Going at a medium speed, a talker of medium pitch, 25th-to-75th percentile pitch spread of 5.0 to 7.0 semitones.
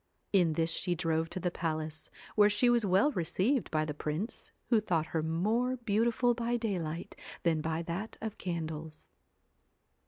Yes: average, 160 wpm; medium, 180 Hz; wide, 5.5 semitones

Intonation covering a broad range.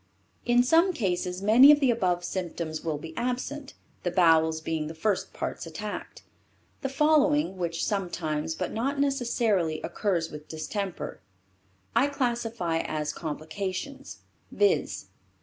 Yes: wide, 7.9 semitones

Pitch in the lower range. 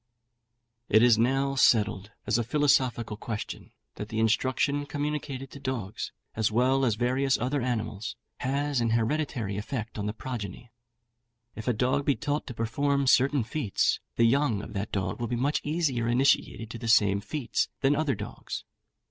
Yes: low, 120 Hz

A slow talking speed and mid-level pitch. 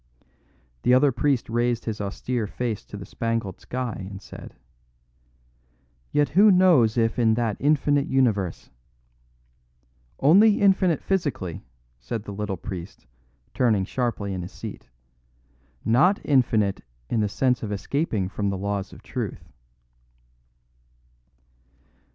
No: slow, 125 wpm; low, 115 Hz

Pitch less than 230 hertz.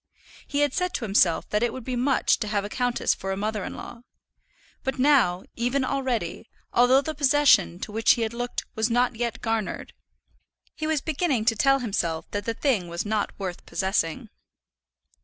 No: high, 235 Hz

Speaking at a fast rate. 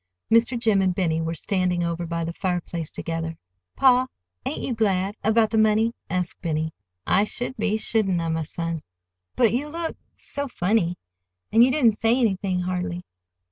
No: average, 160 wpm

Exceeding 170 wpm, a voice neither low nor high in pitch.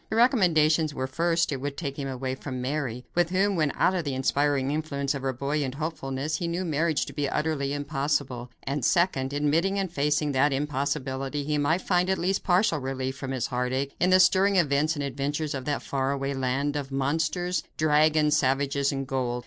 Yes: average, 195 wpm; medium, 145 Hz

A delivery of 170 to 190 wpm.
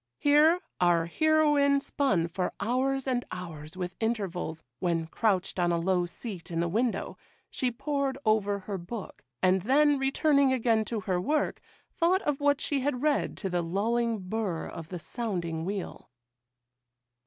No: average, 155 wpm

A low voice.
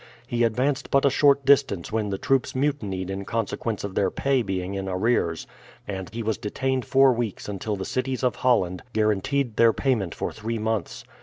Yes: low, 110 Hz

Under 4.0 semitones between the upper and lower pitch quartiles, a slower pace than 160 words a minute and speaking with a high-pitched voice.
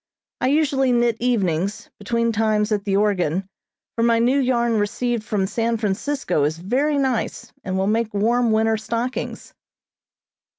Yes: average, 3.0 semitones; average, 145 wpm; high, 225 Hz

